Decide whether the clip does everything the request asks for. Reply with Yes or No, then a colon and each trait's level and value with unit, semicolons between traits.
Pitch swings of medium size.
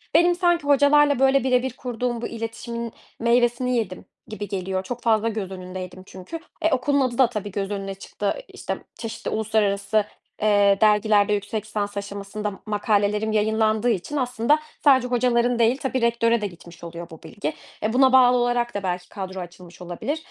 Yes: average, 3.7 semitones